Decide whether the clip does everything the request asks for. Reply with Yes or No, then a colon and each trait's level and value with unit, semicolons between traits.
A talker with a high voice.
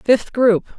Yes: high, 225 Hz